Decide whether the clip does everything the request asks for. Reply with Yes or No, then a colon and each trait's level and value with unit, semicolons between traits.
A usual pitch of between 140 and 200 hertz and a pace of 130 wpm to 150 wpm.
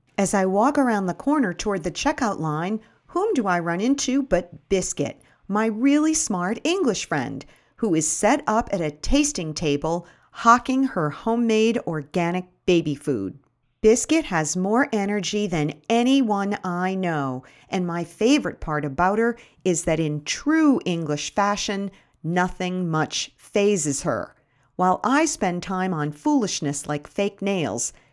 Yes: medium, 185 Hz; average, 145 wpm